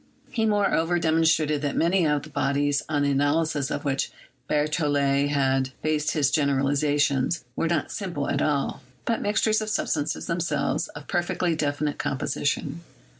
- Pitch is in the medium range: Yes, medium, 150 Hz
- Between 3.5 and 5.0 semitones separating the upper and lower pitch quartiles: No, narrow, 2.6 semitones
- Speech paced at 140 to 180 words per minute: Yes, average, 150 wpm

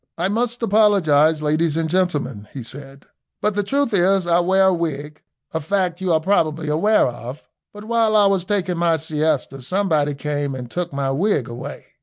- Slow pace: No, average, 185 wpm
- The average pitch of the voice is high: No, medium, 165 Hz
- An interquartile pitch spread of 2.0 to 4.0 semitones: No, average, 5.0 semitones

